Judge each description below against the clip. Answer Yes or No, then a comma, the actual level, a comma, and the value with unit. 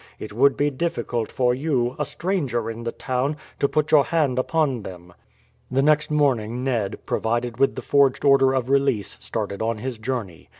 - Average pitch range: Yes, average, 3.3 semitones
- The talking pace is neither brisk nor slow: Yes, average, 180 wpm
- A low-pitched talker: Yes, low, 130 Hz